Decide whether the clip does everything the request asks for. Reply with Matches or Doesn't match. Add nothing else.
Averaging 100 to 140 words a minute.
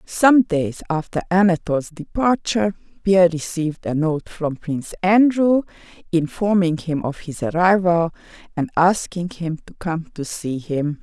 Matches